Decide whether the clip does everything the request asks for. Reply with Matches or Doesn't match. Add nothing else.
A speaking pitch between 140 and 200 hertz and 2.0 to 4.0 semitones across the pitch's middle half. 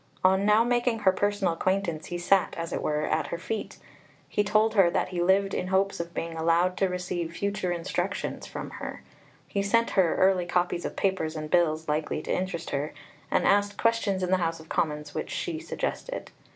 Matches